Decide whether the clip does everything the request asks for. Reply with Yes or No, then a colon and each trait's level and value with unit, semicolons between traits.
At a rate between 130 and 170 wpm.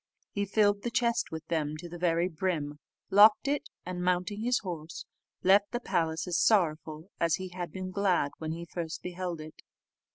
No: average, 185 wpm